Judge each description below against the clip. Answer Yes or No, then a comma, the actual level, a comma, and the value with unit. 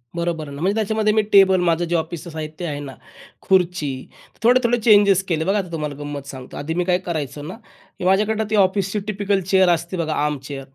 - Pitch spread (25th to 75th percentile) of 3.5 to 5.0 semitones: Yes, average, 4.3 semitones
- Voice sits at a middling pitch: Yes, medium, 175 Hz